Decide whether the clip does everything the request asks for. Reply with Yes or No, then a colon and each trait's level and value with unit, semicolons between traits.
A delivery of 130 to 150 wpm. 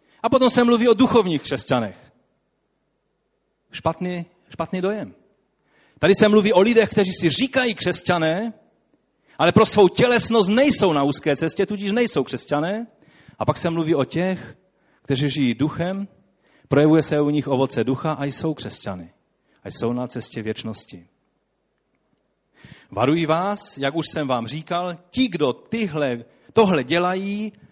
Yes: average, 140 wpm